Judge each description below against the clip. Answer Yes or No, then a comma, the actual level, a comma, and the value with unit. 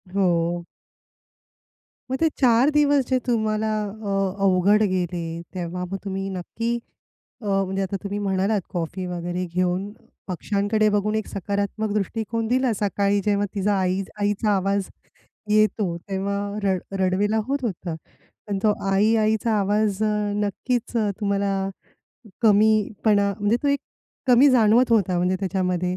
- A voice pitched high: Yes, high, 200 Hz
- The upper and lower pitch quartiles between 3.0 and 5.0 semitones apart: No, narrow, 2.5 semitones